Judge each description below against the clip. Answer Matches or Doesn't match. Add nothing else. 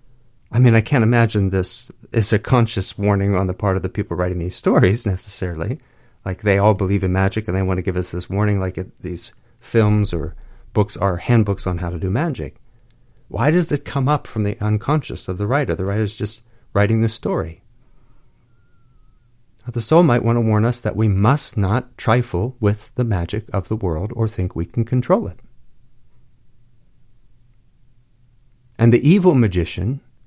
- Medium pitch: Doesn't match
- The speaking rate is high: Doesn't match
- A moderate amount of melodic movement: Matches